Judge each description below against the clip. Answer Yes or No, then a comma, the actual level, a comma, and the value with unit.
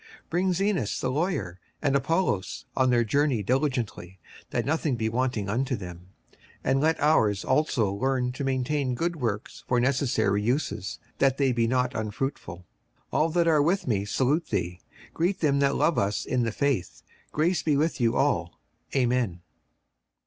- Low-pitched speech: Yes, low, 130 Hz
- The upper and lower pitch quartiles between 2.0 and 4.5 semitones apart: No, average, 5.2 semitones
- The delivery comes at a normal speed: Yes, average, 170 wpm